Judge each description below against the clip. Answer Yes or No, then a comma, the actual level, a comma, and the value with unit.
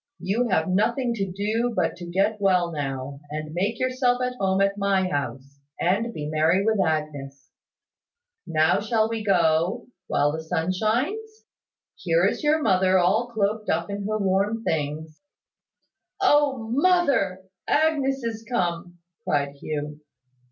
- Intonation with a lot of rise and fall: Yes, wide, 6.1 semitones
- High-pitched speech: Yes, high, 195 Hz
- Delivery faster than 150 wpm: No, average, 145 wpm